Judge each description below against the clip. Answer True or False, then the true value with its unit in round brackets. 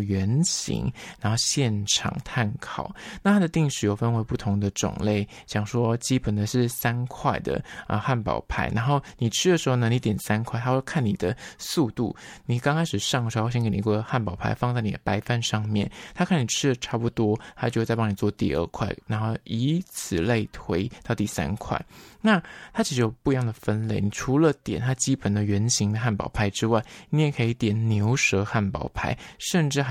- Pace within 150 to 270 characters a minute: False (290 characters per minute)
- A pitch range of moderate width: True (3.9 semitones)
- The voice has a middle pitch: False (115 Hz)